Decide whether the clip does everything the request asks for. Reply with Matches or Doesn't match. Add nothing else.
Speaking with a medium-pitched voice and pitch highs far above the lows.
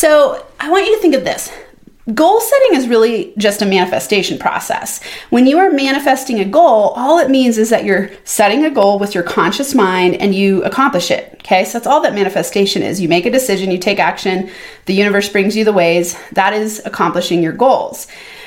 Doesn't match